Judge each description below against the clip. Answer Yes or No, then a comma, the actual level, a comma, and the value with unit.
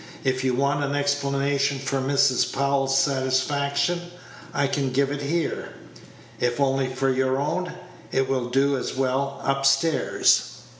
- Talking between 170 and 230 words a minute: No, average, 145 wpm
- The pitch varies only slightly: Yes, narrow, 1.2 semitones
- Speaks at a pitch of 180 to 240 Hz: No, low, 135 Hz